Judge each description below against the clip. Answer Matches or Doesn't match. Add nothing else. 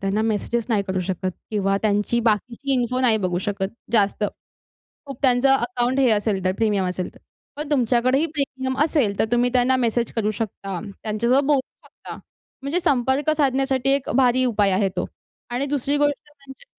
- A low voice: Doesn't match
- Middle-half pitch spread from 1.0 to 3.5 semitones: Doesn't match